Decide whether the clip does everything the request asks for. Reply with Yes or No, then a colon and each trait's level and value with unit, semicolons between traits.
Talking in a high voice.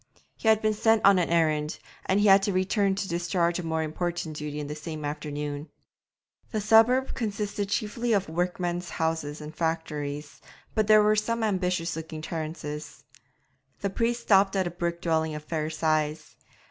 No: medium, 170 Hz